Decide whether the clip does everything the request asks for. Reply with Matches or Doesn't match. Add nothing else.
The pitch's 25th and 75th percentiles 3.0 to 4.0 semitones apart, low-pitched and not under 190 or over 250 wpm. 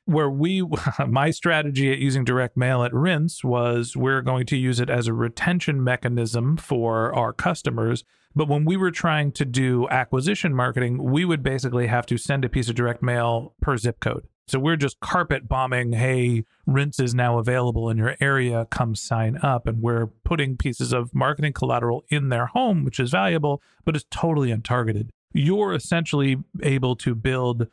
Doesn't match